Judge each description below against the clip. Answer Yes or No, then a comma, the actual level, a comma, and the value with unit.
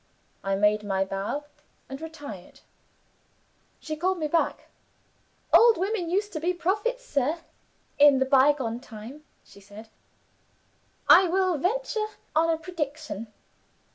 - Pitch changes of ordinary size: No, wide, 7.9 semitones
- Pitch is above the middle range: Yes, very high, 305 Hz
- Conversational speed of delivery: No, slow, 125 wpm